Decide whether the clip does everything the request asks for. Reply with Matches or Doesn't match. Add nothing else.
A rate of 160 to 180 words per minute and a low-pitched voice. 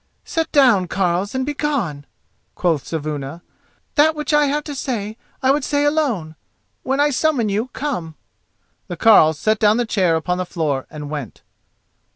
Doesn't match